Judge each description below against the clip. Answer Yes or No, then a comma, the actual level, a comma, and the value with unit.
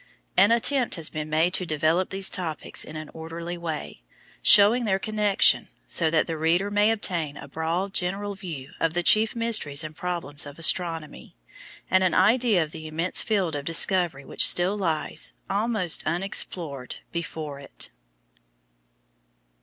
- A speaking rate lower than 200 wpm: Yes, average, 155 wpm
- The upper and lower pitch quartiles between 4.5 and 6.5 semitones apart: No, average, 3.9 semitones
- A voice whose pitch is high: No, medium, 170 Hz